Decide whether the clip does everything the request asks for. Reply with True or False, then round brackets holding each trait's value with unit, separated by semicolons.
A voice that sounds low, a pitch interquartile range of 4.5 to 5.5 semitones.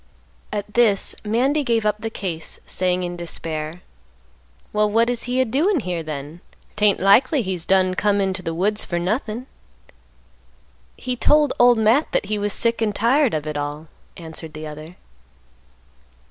False (205 Hz; 5.2 semitones)